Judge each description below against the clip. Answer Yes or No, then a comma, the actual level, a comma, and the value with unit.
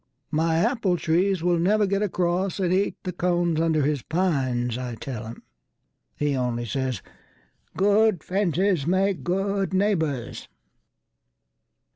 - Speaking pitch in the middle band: Yes, medium, 175 Hz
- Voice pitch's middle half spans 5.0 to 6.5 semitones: Yes, wide, 5.6 semitones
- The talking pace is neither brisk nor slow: No, slow, 115 wpm